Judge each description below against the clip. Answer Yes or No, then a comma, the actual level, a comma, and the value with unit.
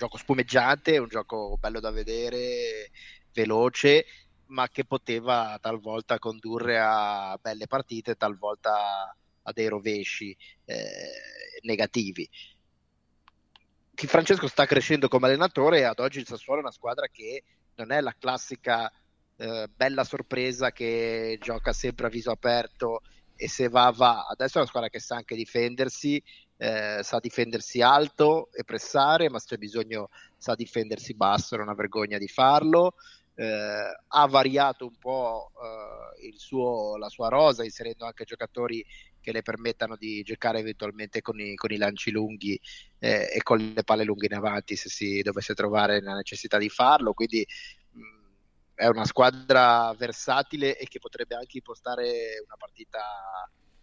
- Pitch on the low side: Yes, low, 115 Hz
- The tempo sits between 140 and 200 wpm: Yes, average, 150 wpm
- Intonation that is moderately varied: Yes, average, 3.3 semitones